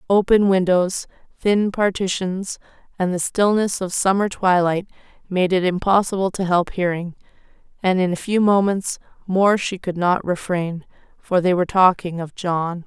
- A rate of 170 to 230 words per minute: No, average, 150 wpm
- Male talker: No, female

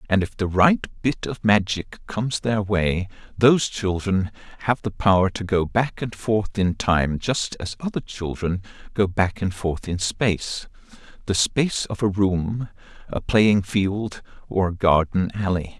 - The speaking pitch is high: No, low, 100 Hz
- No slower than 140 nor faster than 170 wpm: Yes, average, 165 wpm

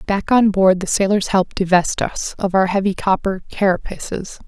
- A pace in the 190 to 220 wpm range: No, average, 175 wpm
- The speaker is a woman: Yes, female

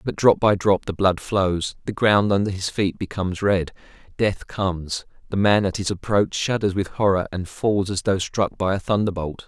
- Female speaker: No, male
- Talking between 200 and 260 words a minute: Yes, fast, 205 wpm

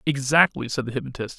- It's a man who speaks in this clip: Yes, male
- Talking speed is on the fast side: No, average, 175 wpm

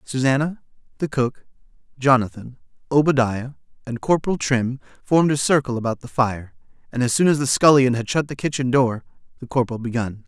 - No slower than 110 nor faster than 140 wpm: No, average, 160 wpm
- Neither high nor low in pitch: No, low, 130 Hz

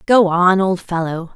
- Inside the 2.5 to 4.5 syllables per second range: Yes, 4.1 syllables/s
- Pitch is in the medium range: Yes, medium, 180 Hz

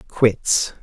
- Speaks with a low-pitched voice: Yes, low, 115 Hz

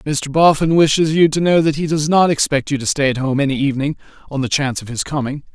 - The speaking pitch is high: No, medium, 145 Hz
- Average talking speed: No, fast, 260 wpm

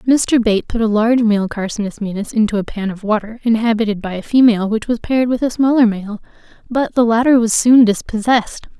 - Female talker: Yes, female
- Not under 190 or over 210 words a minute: Yes, fast, 205 wpm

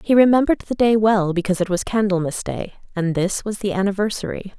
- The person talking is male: No, female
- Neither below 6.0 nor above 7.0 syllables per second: Yes, 6.1 syllables/s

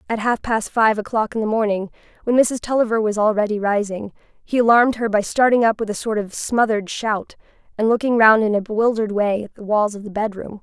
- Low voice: No, high, 215 Hz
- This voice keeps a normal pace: No, fast, 220 wpm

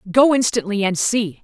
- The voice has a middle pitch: No, high, 215 Hz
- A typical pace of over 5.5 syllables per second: No, 5.0 syllables/s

